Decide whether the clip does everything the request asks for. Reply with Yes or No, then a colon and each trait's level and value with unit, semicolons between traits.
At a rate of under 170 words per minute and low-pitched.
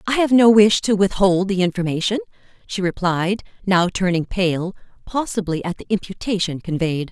No: average, 150 wpm; high, 195 Hz